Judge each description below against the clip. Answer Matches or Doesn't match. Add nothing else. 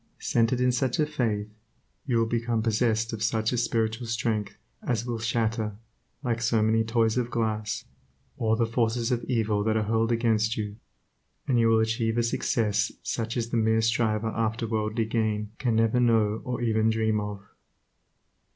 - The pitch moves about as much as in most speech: Doesn't match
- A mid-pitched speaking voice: Doesn't match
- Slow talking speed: Doesn't match